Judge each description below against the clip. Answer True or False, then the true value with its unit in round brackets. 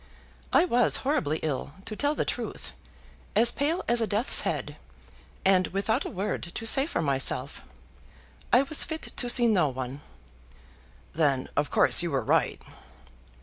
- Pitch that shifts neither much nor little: False (8.9 semitones)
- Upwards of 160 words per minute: False (155 wpm)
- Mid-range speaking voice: False (210 Hz)